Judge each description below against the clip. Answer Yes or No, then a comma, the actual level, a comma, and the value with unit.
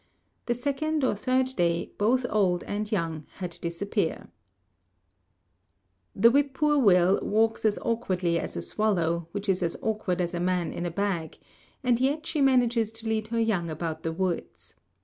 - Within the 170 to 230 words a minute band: No, average, 160 wpm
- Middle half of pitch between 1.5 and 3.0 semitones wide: No, average, 5.3 semitones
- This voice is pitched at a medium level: No, high, 205 Hz